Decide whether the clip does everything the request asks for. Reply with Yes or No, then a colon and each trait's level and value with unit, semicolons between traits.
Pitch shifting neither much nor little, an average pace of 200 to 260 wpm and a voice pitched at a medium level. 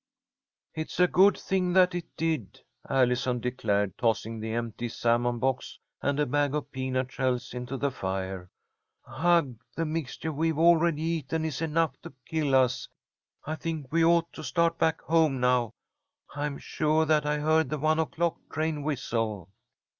No: average, 4.5 semitones; average, 160 wpm; medium, 145 Hz